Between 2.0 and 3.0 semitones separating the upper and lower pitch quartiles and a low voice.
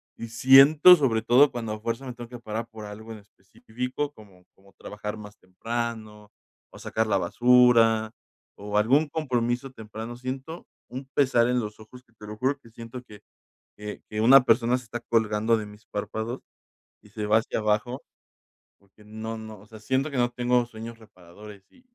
Yes: average, 2.7 semitones; low, 115 Hz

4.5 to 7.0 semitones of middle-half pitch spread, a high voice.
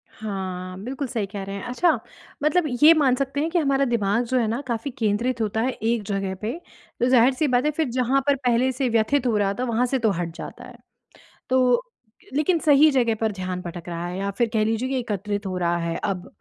Yes: average, 4.9 semitones; high, 235 Hz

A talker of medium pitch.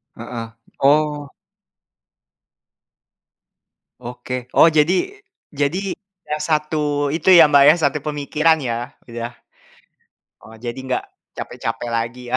Yes: medium, 145 Hz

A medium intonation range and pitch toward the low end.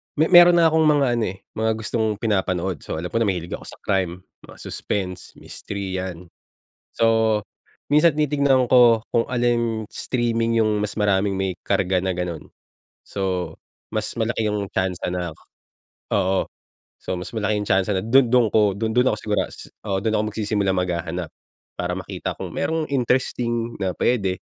Yes: average, 3.9 semitones; low, 105 Hz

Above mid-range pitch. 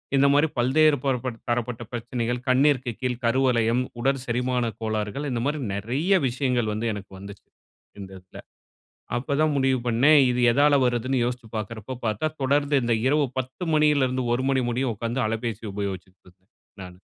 No: low, 125 Hz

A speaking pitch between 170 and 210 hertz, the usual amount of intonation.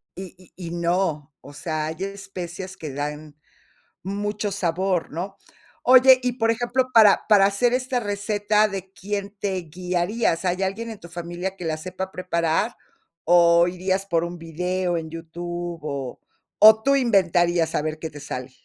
Yes: medium, 185 Hz; average, 3.3 semitones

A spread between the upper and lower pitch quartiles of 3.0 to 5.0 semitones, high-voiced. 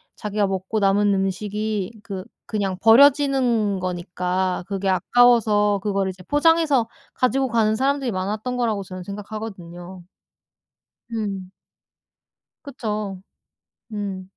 Yes: average, 3.3 semitones; high, 205 Hz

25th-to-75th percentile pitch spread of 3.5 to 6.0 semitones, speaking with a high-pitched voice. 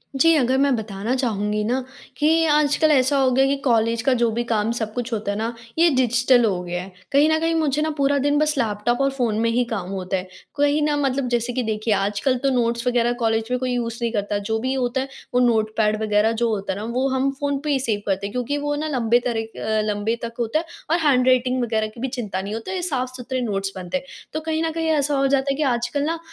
Yes: average, 4.0 semitones; high, 245 Hz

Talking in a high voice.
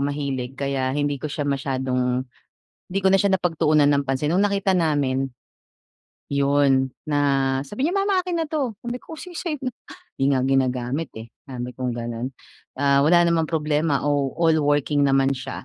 No: medium, 145 Hz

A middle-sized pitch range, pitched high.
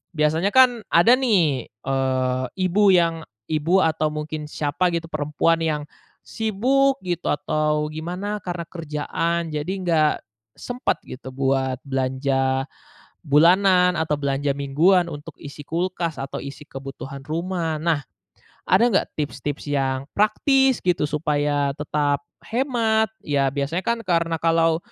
No: average, 4.0 semitones; medium, 160 Hz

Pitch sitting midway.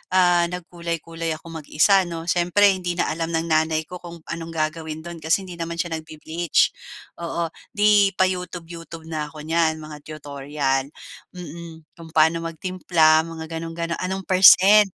Yes: medium, 165 Hz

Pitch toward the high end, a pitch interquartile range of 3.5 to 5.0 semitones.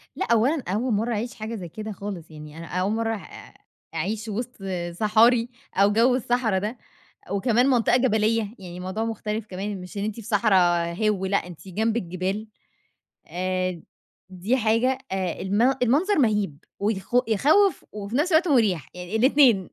Yes: high, 215 Hz; average, 3.8 semitones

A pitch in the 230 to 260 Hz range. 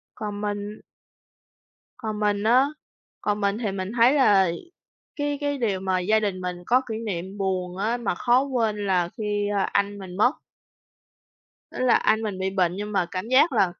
No: high, 205 Hz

